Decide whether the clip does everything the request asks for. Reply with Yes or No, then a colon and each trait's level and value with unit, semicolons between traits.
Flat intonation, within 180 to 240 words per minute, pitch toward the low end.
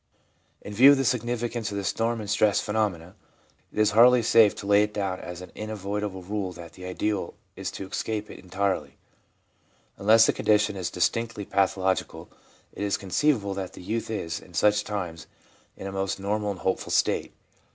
Yes: narrow, 2.3 semitones; average, 185 wpm; low, 105 Hz